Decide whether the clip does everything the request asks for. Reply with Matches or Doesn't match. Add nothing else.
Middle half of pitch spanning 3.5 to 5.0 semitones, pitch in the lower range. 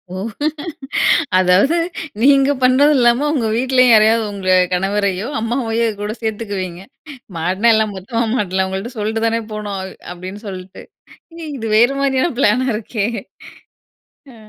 Doesn't match